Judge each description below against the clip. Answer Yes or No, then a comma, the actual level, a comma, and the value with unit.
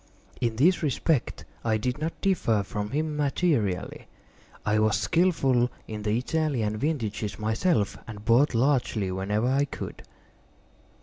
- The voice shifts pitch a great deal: Yes, wide, 5.7 semitones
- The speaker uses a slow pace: Yes, slow, 130 wpm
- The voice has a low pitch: Yes, low, 120 Hz